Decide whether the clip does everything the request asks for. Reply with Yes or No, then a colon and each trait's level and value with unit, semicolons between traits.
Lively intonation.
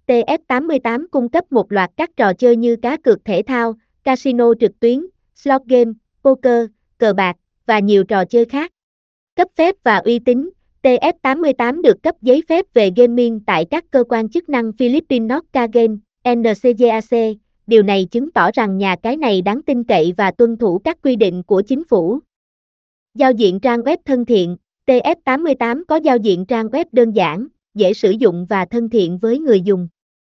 No: average, 3.9 semitones